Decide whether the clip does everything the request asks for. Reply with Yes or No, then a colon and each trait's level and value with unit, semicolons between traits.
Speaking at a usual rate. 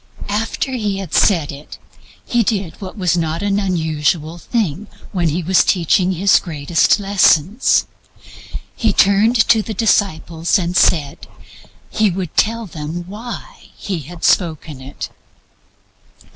No: slow, 130 wpm